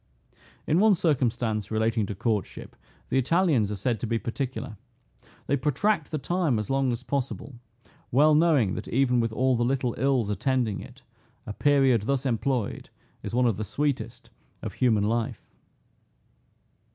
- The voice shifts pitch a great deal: No, average, 3.7 semitones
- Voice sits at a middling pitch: No, low, 125 Hz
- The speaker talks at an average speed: Yes, average, 155 wpm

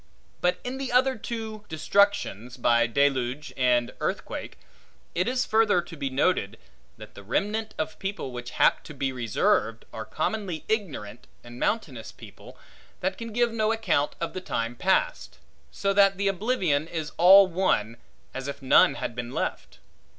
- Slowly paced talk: No, average, 160 wpm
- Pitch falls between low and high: Yes, medium, 170 Hz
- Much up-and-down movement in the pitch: Yes, wide, 8.8 semitones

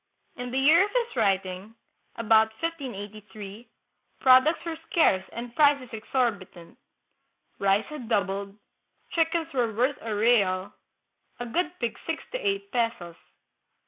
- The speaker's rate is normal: No, slow, 125 wpm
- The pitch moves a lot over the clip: Yes, wide, 6.8 semitones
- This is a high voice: Yes, high, 235 Hz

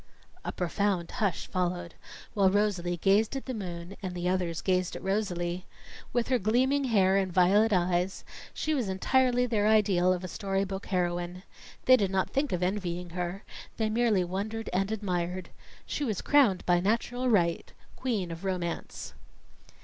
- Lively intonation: No, average, 3.4 semitones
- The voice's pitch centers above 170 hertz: Yes, high, 190 Hz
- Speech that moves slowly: No, average, 160 wpm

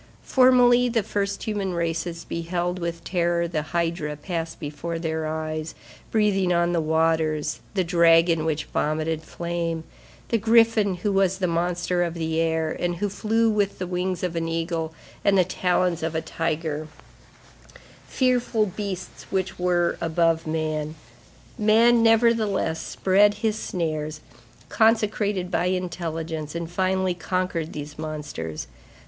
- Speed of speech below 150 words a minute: Yes, slow, 135 wpm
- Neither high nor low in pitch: Yes, medium, 170 Hz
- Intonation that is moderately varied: Yes, average, 3.2 semitones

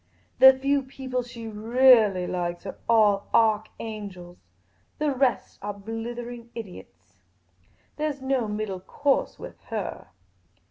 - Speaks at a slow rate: Yes, slow, 125 wpm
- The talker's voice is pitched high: Yes, high, 225 Hz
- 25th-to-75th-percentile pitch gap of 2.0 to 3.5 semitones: No, average, 4.2 semitones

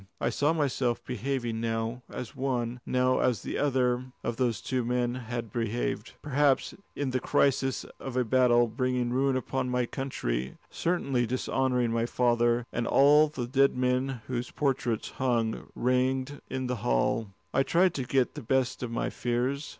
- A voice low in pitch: Yes, low, 125 Hz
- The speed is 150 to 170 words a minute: Yes, average, 165 wpm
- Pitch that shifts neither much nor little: No, narrow, 1.9 semitones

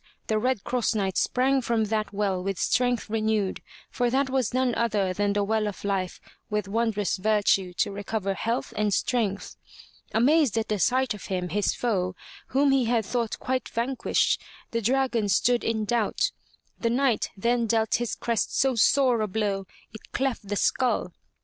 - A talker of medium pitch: No, high, 220 Hz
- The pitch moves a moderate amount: Yes, average, 3.3 semitones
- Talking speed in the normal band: Yes, average, 170 wpm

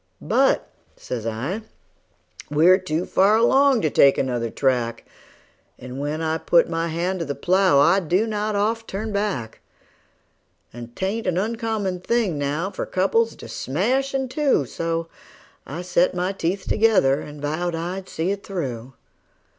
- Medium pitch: Yes, medium, 180 Hz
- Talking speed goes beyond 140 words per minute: Yes, average, 155 wpm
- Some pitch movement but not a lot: No, wide, 5.9 semitones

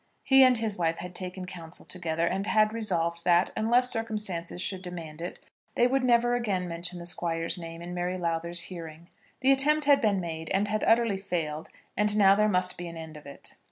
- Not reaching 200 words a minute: No, fast, 205 wpm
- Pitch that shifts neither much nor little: Yes, average, 4.2 semitones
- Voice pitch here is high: No, medium, 180 Hz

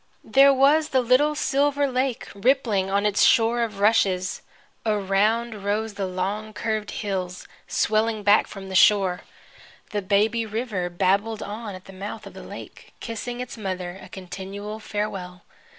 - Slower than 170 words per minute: Yes, average, 150 wpm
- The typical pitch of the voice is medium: No, high, 210 Hz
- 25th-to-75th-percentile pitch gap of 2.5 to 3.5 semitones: Yes, average, 3.1 semitones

